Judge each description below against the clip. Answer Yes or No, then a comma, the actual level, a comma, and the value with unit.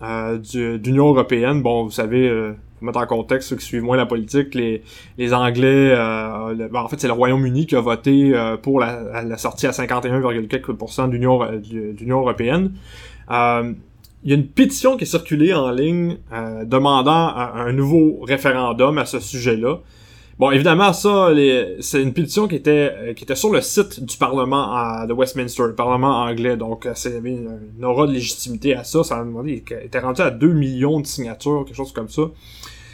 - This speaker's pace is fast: No, average, 200 wpm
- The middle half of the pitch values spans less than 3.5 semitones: Yes, average, 3.0 semitones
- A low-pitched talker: Yes, low, 125 Hz